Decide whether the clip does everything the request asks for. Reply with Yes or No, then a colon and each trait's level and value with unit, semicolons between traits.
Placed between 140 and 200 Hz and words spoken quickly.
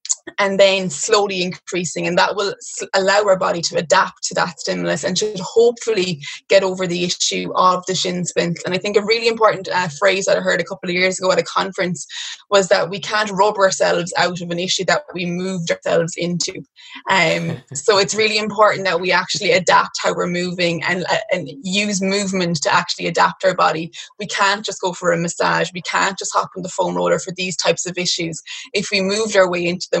Yes: medium, 185 Hz; fast, 220 wpm